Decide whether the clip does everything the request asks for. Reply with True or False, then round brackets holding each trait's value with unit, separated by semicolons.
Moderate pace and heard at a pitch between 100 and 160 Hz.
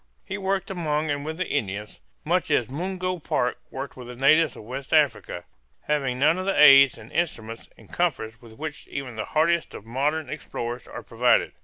True (185 wpm; 140 Hz)